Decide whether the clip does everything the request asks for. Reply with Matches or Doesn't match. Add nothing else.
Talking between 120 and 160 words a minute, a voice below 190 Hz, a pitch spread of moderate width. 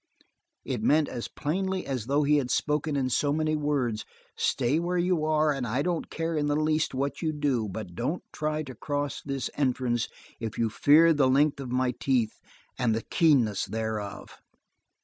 Doesn't match